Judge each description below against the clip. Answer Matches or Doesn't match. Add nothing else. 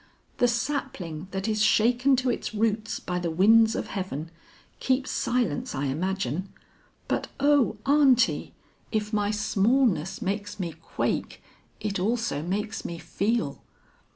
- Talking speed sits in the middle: Doesn't match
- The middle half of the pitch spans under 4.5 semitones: Doesn't match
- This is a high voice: Matches